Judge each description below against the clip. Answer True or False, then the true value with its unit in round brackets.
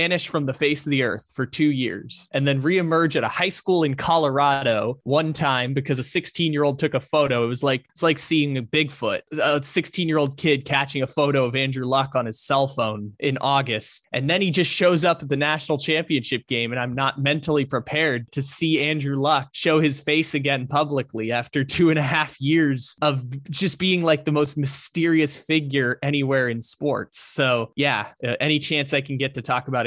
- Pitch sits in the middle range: True (145 Hz)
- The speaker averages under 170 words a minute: False (205 wpm)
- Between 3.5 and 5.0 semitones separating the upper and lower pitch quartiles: False (2.9 semitones)